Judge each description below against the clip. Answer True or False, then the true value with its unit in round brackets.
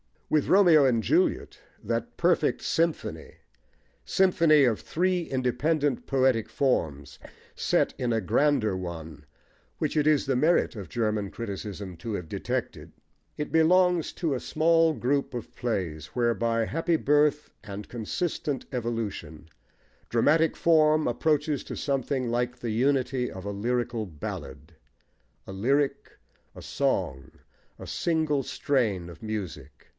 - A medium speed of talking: False (130 wpm)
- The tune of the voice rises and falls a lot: True (6.4 semitones)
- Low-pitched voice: True (125 Hz)